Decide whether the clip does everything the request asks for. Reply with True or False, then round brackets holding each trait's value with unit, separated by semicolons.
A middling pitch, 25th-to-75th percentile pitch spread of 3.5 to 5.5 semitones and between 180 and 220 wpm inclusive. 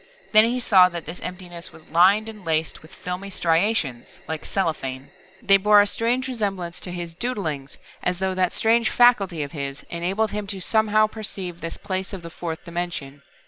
True (180 Hz; 4.0 semitones; 185 wpm)